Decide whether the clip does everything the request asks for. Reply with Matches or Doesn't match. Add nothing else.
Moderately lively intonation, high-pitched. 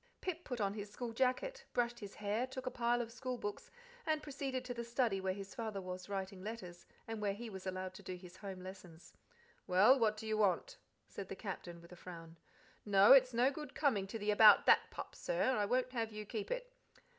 Matches